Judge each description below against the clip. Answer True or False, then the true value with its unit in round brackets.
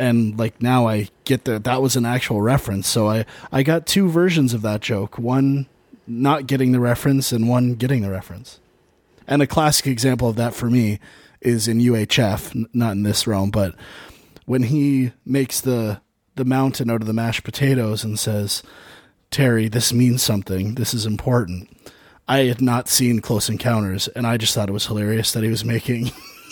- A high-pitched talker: False (120 Hz)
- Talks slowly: False (190 wpm)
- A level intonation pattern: False (3.0 semitones)